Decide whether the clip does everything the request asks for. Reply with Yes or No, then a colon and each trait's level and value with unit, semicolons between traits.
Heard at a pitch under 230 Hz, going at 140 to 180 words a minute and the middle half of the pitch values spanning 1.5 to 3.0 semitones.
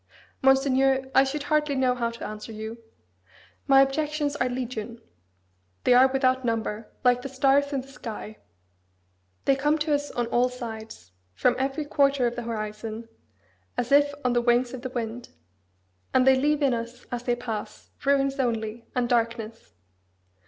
No: very high, 250 Hz; average, 165 wpm; average, 2.7 semitones